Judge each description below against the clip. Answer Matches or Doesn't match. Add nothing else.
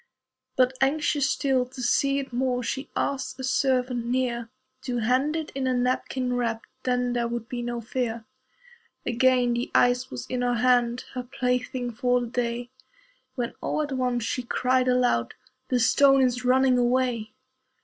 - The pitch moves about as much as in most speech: Doesn't match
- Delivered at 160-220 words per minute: Matches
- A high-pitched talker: Matches